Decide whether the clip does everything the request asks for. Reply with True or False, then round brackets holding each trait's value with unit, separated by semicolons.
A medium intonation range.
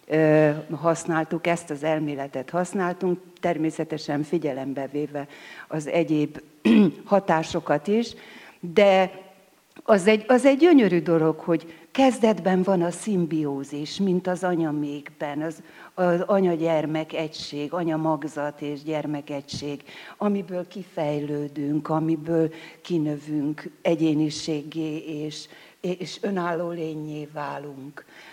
True (3.1 semitones)